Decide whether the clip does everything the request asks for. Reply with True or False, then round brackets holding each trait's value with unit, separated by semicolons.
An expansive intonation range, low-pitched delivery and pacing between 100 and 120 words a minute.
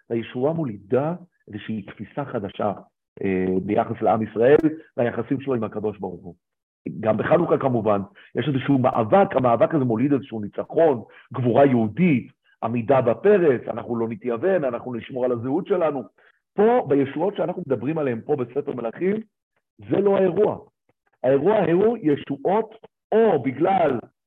False (5.9 semitones; 130 Hz; 135 wpm)